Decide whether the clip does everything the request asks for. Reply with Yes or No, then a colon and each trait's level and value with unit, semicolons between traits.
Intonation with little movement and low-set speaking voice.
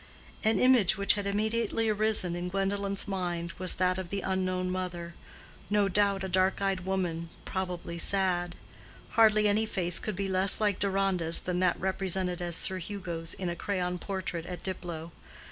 No: narrow, 2.1 semitones; high, 190 Hz